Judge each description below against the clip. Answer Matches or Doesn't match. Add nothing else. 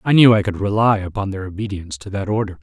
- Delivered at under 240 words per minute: Doesn't match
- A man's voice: Matches